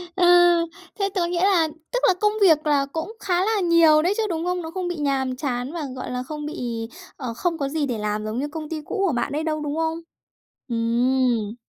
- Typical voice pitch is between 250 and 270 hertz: No, very high, 305 Hz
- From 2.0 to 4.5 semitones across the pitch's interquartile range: No, average, 5.3 semitones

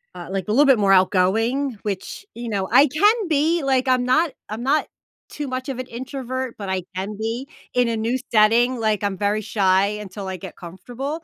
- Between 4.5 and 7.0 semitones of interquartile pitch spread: Yes, average, 4.8 semitones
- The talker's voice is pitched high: Yes, high, 235 Hz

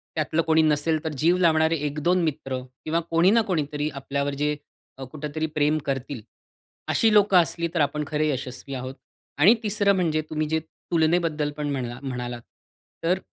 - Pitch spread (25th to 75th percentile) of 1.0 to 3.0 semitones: Yes, average, 2.7 semitones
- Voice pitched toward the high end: No, medium, 155 Hz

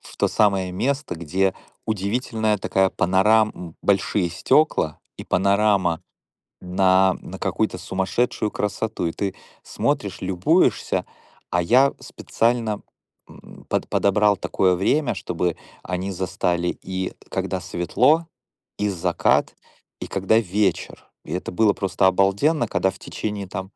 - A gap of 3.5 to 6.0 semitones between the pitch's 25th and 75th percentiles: No, average, 2.8 semitones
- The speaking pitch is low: Yes, very low, 95 Hz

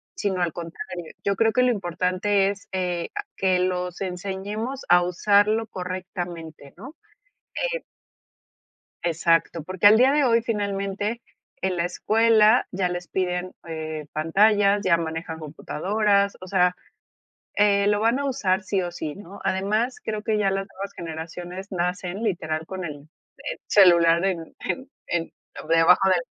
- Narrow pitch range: No, average, 3.0 semitones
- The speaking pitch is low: No, high, 190 Hz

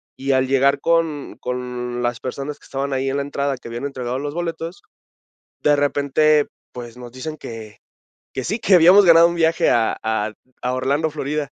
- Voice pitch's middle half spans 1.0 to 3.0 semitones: No, average, 3.5 semitones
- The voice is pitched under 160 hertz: Yes, medium, 140 Hz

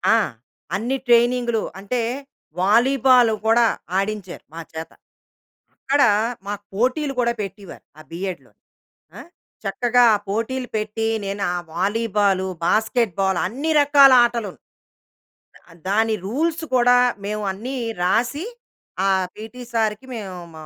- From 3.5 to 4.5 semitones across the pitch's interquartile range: Yes, average, 3.8 semitones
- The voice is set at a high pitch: Yes, high, 225 Hz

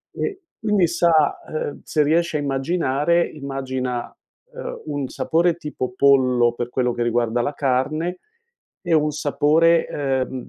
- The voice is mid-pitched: Yes, medium, 145 Hz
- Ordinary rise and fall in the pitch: Yes, average, 4.1 semitones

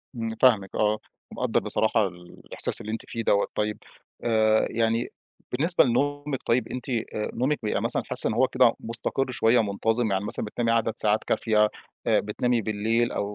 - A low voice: Yes, low, 115 Hz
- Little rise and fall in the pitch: Yes, narrow, 2.2 semitones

